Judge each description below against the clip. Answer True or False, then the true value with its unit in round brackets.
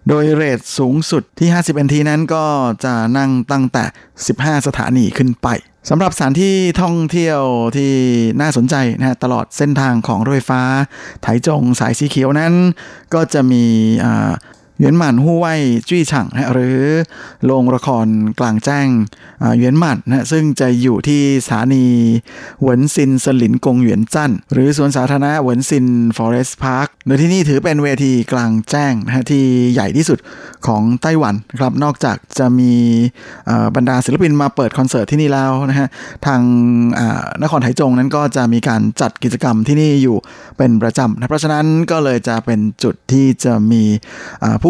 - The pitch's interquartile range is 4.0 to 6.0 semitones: False (3.2 semitones)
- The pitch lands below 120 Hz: False (130 Hz)